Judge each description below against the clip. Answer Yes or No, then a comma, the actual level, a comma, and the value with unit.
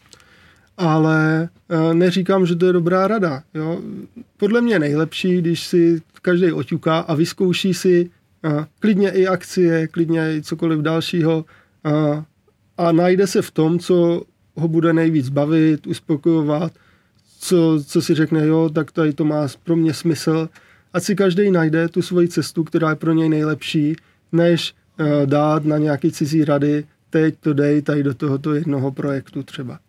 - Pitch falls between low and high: Yes, medium, 160 Hz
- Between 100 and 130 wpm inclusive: No, average, 160 wpm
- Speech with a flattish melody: Yes, narrow, 2.3 semitones